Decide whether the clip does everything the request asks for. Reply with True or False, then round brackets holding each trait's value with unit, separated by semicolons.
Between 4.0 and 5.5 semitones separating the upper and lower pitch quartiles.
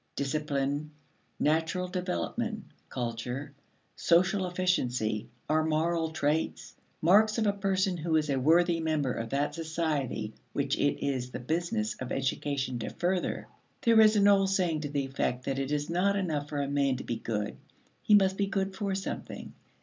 True (5.2 semitones)